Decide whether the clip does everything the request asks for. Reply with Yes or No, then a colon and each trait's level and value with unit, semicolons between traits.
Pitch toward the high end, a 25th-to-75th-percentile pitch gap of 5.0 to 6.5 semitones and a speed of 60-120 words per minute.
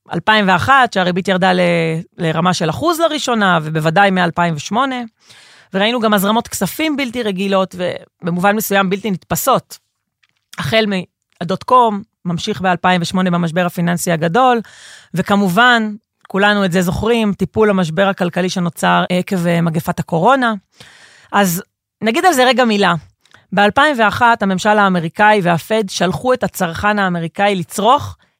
No: high, 195 Hz; average, 3.6 semitones; average, 115 wpm